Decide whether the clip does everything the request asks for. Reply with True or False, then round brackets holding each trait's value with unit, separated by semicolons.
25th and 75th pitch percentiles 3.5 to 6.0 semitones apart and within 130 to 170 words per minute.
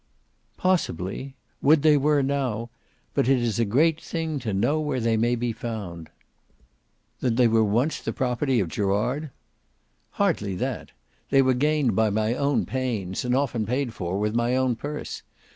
True (4.4 semitones; 165 wpm)